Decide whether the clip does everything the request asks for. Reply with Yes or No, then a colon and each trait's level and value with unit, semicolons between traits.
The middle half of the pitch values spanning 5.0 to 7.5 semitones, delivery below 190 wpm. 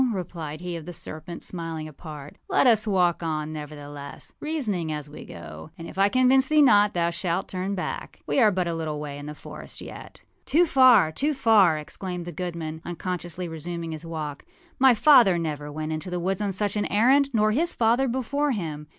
No: wide, 5.6 semitones; average, 200 wpm